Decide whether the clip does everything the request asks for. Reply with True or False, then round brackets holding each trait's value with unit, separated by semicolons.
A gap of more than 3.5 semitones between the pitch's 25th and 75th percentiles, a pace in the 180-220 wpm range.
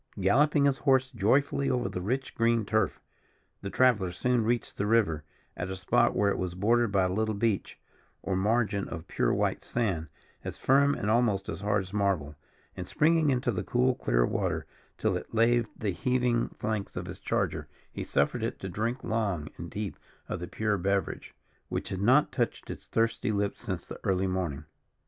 True (4.1 semitones; 190 wpm)